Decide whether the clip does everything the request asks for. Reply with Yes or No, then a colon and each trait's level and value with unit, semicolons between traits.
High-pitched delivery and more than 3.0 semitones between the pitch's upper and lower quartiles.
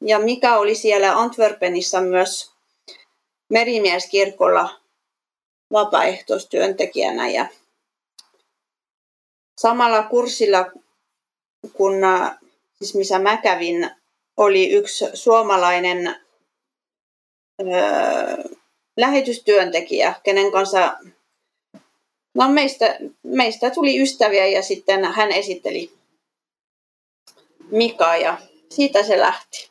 Yes: high, 210 Hz; average, 4.4 semitones